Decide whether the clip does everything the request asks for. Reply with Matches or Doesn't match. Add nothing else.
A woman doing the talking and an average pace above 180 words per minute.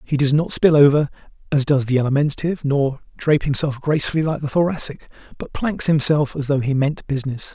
Doesn't match